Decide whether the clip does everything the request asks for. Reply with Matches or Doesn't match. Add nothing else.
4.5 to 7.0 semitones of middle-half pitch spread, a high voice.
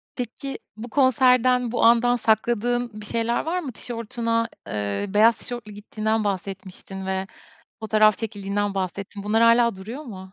Doesn't match